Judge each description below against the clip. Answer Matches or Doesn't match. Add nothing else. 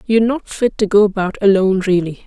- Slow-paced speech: Doesn't match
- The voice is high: Matches